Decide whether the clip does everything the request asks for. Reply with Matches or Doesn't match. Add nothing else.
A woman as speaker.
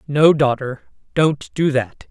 Matches